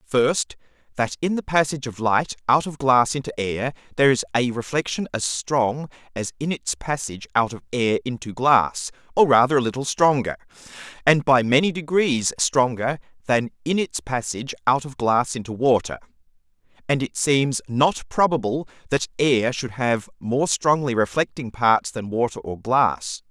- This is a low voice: Yes, low, 130 Hz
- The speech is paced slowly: No, average, 160 wpm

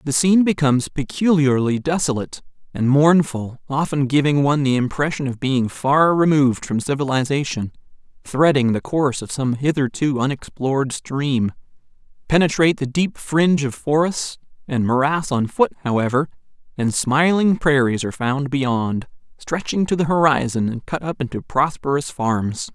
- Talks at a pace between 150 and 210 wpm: No, average, 140 wpm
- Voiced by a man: Yes, male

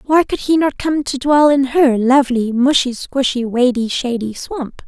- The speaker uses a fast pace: No, average, 185 wpm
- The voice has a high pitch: Yes, very high, 265 Hz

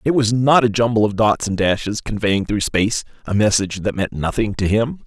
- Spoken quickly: Yes, fast, 225 wpm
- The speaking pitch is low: Yes, low, 110 Hz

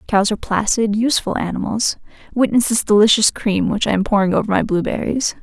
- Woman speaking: Yes, female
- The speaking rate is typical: Yes, average, 165 wpm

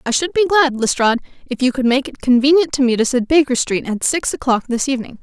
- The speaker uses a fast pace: Yes, fast, 255 wpm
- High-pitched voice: Yes, very high, 260 Hz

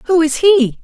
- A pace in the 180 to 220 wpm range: Yes, fast, 215 wpm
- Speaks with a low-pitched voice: No, very high, 320 Hz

